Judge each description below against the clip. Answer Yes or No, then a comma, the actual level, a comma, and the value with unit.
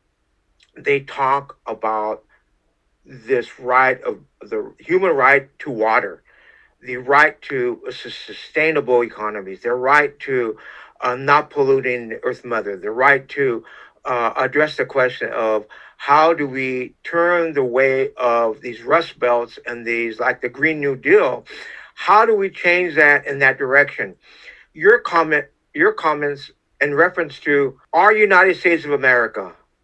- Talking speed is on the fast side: No, average, 140 wpm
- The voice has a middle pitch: Yes, medium, 155 Hz